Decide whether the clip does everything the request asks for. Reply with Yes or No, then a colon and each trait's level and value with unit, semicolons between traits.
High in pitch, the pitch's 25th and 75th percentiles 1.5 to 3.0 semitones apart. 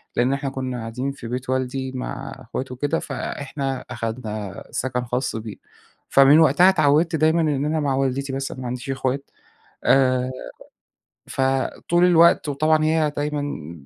No: low, 135 Hz; narrow, 2.6 semitones